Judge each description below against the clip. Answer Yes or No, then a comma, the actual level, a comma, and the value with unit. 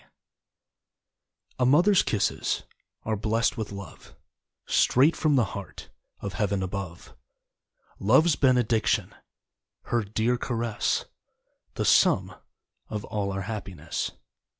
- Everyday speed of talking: No, slow, 105 wpm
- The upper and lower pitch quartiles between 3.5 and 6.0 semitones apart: Yes, average, 3.8 semitones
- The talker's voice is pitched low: Yes, low, 110 Hz